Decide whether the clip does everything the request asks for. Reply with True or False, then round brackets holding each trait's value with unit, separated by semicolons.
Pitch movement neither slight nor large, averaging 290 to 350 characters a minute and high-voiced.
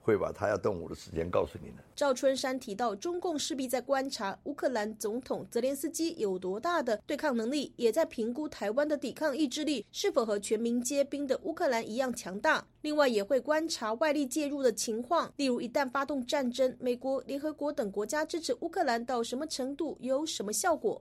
True (4.3 semitones; 325 characters per minute; 275 Hz)